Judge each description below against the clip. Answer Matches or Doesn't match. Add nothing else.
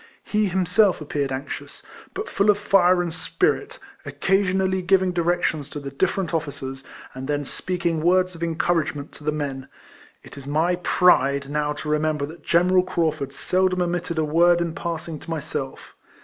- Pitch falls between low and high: Matches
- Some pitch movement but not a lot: Matches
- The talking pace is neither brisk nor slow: Matches